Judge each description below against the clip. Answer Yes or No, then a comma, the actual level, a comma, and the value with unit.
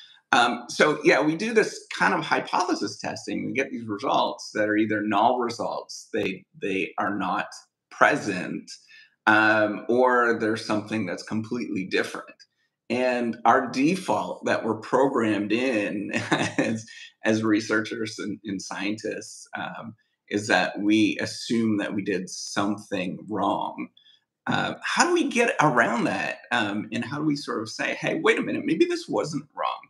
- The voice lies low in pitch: Yes, low, 115 Hz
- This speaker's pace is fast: No, average, 155 wpm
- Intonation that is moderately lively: No, wide, 7.9 semitones